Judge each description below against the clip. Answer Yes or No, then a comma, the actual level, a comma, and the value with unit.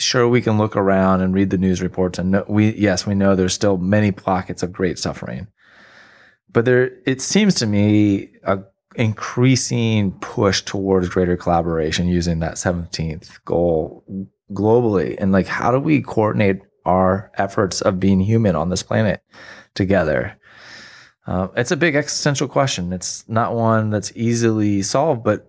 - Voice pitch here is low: Yes, low, 100 Hz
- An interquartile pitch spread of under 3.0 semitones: No, average, 3.7 semitones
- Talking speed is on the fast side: No, average, 160 wpm